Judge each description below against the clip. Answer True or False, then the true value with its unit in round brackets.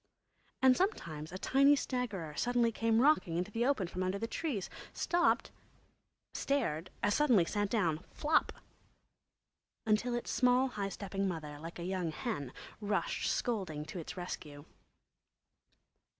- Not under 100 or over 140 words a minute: True (135 wpm)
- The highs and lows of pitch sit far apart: True (6.5 semitones)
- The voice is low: False (205 Hz)